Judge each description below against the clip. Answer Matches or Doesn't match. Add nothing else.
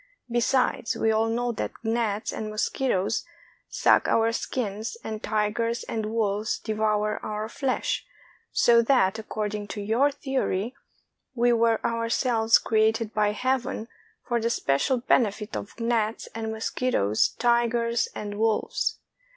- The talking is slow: Matches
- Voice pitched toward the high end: Matches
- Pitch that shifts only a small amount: Matches